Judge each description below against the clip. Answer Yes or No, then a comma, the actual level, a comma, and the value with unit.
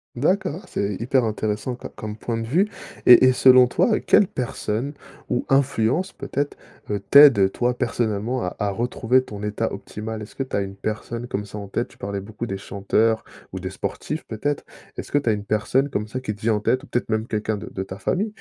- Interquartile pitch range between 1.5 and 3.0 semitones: No, average, 3.7 semitones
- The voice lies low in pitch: Yes, low, 115 Hz